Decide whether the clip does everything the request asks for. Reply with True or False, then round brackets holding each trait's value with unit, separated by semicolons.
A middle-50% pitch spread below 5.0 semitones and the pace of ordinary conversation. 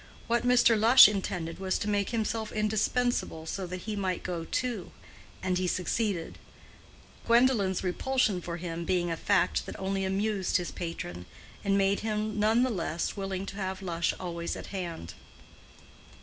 True (3.4 semitones; 160 wpm)